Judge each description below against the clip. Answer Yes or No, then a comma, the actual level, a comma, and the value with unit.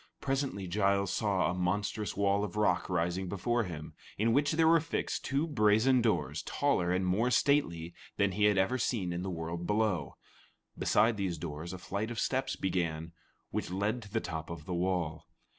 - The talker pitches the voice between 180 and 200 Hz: No, low, 100 Hz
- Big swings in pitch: No, average, 4.2 semitones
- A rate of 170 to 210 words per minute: Yes, average, 180 wpm